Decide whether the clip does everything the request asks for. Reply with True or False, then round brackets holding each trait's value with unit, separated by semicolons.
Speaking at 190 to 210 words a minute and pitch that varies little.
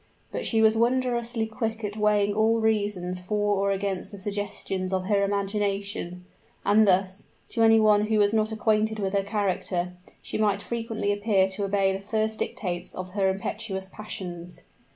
False (170 wpm; 2.1 semitones)